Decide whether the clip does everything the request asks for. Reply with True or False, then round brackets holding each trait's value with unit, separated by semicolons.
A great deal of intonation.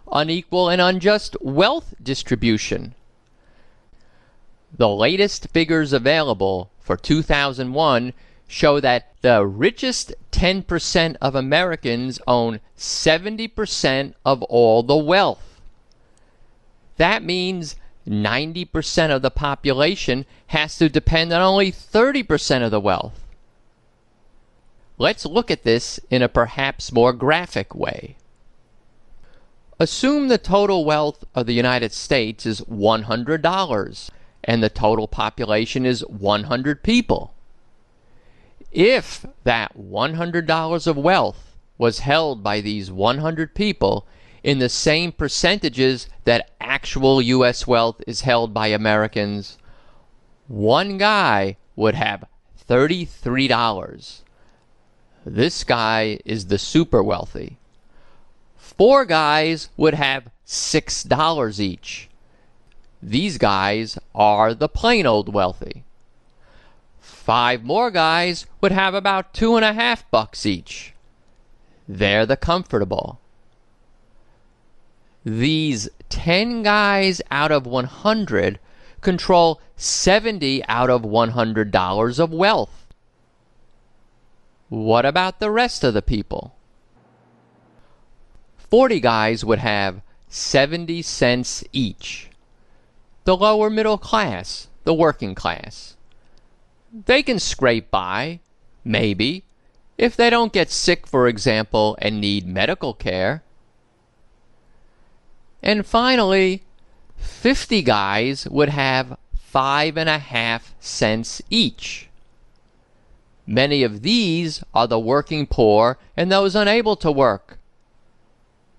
True (7.3 semitones)